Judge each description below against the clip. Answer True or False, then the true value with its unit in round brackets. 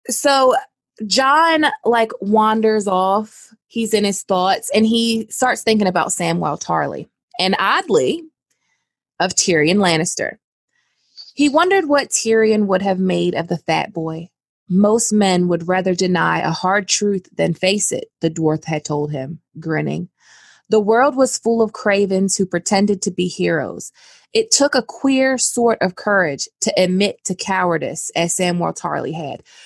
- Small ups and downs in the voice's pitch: False (4.4 semitones)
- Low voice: False (200 Hz)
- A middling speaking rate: True (150 wpm)